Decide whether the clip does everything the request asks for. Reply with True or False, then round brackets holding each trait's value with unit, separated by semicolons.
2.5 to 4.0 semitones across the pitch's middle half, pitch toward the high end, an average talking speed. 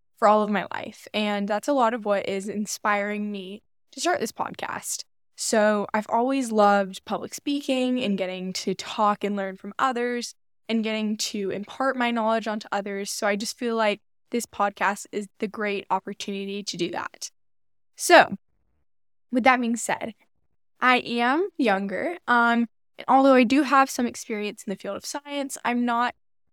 True (3.4 semitones; 215 Hz; 175 wpm)